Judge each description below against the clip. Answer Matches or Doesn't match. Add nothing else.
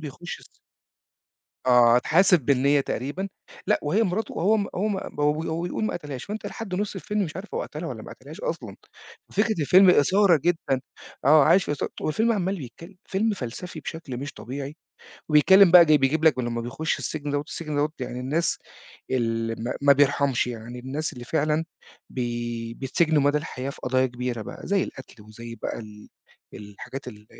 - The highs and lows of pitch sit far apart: Matches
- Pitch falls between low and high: Matches